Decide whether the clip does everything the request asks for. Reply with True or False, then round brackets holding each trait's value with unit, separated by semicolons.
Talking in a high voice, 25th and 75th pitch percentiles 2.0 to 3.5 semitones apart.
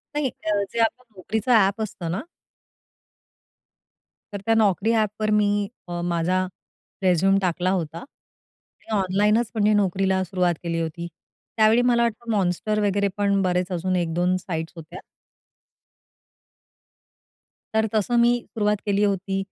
True (195 Hz; 3.0 semitones)